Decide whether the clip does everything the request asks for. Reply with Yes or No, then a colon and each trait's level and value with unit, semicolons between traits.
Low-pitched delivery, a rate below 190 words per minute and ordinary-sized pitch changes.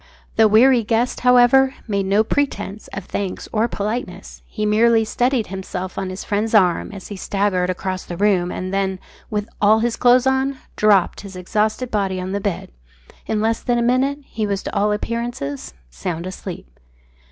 No: high, 210 Hz; average, 175 wpm; average, 3.7 semitones